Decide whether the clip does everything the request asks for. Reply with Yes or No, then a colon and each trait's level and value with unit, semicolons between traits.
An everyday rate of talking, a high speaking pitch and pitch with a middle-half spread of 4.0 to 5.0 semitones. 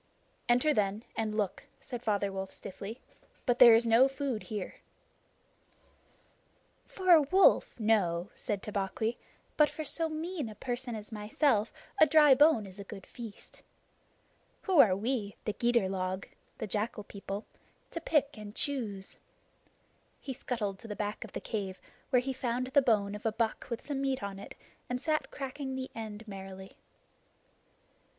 Yes: average, 160 wpm; high, 225 Hz; average, 4.5 semitones